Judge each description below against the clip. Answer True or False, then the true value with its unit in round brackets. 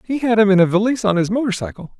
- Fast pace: True (300 wpm)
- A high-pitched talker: True (205 Hz)